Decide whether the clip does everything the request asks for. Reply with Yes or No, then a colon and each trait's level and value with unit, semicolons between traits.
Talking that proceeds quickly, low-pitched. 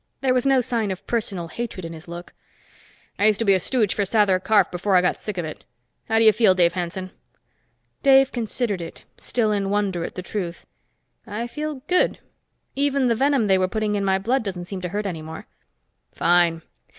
No: fast, 210 wpm; high, 205 Hz